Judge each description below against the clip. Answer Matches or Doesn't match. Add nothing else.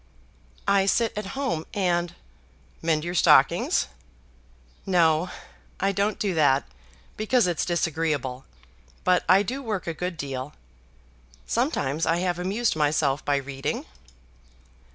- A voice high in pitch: Doesn't match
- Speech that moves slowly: Matches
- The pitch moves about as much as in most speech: Matches